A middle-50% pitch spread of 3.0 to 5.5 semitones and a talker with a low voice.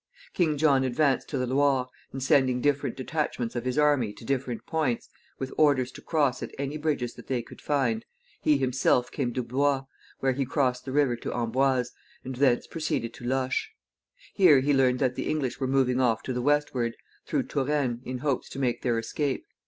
No: narrow, 2.4 semitones; low, 130 Hz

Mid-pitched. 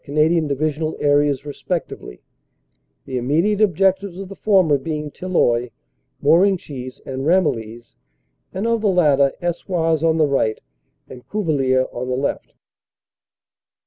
Yes: medium, 155 Hz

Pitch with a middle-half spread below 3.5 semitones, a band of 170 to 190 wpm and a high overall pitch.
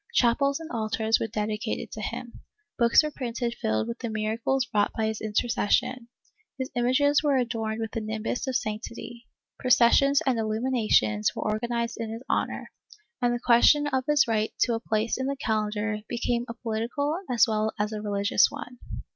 Yes: narrow, 2.6 semitones; average, 175 wpm; high, 230 Hz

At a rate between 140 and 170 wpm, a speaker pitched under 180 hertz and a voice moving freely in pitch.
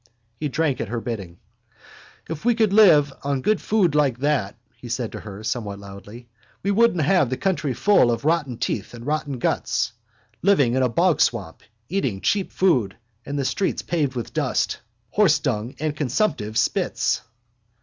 Yes: average, 165 wpm; low, 135 Hz; wide, 6.4 semitones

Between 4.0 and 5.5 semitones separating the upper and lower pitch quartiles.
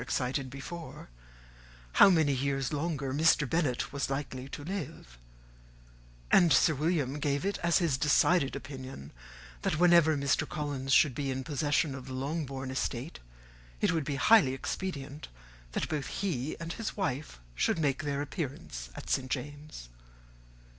No: average, 3.3 semitones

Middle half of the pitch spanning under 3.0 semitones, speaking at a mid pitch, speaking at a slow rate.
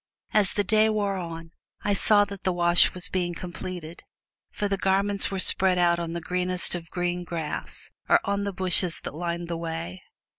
No: narrow, 2.4 semitones; medium, 180 Hz; average, 190 wpm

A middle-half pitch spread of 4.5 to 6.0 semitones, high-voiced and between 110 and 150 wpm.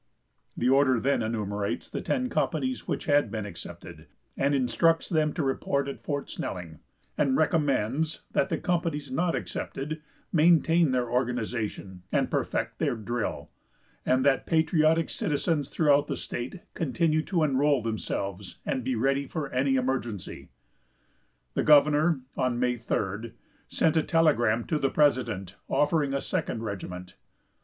No: average, 4.9 semitones; low, 135 Hz; average, 140 wpm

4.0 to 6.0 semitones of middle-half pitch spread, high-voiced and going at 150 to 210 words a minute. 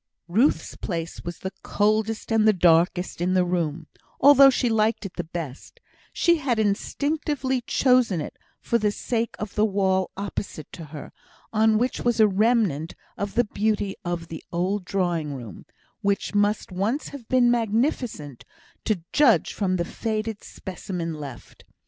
Yes: average, 4.6 semitones; high, 205 Hz; average, 155 wpm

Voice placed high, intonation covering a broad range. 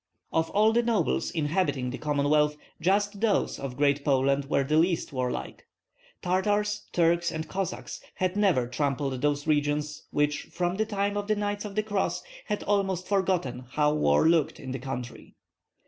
No: medium, 160 Hz; wide, 5.7 semitones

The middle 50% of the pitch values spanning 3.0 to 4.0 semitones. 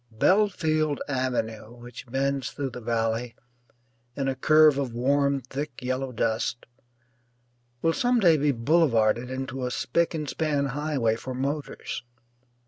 Yes: average, 3.7 semitones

